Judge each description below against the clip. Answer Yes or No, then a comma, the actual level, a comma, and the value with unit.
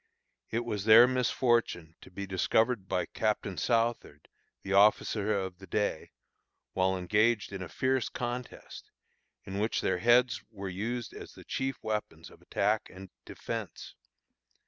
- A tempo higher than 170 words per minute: No, average, 145 wpm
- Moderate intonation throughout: Yes, average, 3.9 semitones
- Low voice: Yes, low, 105 Hz